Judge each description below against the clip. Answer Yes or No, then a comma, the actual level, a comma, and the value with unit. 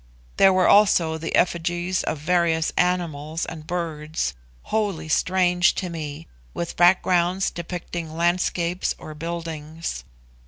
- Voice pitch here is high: No, medium, 170 Hz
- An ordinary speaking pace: No, slow, 115 wpm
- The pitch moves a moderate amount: No, narrow, 1.9 semitones